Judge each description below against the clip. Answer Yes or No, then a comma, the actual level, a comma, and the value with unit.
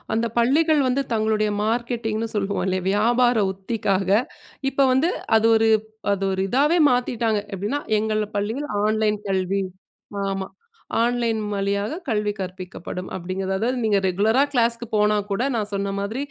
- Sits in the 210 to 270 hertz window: Yes, high, 215 Hz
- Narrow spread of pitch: No, average, 3.2 semitones